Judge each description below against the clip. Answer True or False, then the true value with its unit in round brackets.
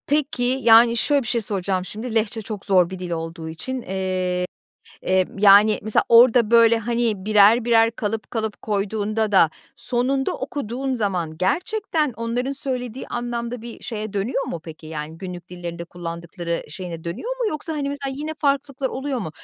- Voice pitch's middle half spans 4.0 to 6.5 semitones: True (5.1 semitones)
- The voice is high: True (220 Hz)